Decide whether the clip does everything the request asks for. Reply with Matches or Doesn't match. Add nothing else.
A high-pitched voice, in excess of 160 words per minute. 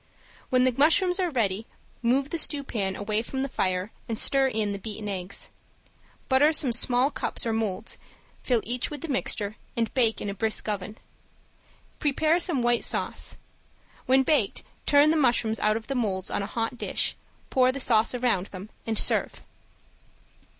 Matches